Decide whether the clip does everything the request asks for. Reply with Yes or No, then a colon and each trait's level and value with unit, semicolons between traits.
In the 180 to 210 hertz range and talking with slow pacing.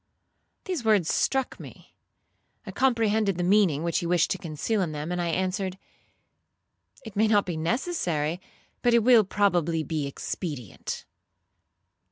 No: medium, 185 Hz; average, 145 wpm